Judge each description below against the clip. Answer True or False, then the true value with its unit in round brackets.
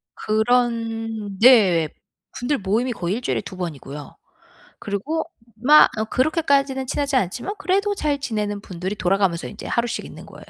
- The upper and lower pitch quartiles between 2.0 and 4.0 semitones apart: False (5.2 semitones)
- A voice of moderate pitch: False (225 Hz)